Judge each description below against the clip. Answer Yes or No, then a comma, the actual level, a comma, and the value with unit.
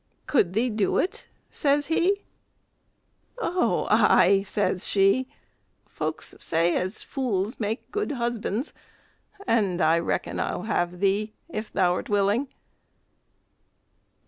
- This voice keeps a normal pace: No, slow, 115 wpm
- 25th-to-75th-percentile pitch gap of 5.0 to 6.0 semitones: Yes, average, 5.3 semitones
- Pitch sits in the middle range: No, high, 215 Hz